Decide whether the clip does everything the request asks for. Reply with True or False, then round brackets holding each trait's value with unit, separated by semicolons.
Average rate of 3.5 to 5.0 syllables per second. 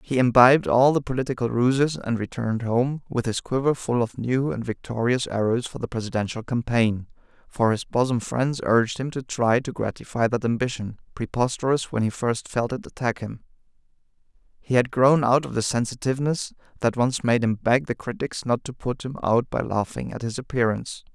False (5.4 syllables/s)